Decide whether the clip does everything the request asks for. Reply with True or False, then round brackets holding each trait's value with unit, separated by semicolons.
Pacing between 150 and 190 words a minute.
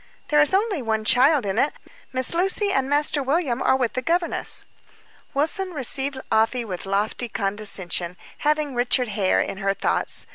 True (160 wpm)